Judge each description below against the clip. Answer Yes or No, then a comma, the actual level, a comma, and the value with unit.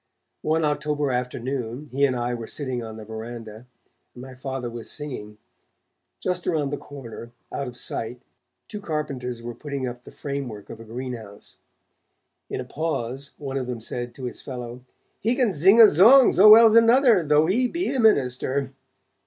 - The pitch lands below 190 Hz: Yes, low, 135 Hz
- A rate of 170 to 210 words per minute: Yes, average, 175 wpm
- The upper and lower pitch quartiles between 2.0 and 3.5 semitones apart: No, average, 4.6 semitones